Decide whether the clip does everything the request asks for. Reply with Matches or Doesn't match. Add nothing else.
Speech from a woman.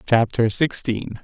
Doesn't match